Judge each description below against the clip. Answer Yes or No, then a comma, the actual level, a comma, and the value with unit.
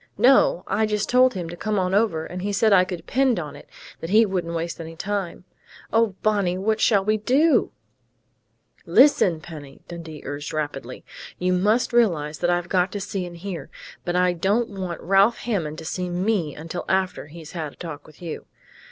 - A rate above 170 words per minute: Yes, average, 195 wpm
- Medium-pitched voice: Yes, medium, 180 Hz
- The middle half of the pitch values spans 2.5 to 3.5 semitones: No, average, 4.0 semitones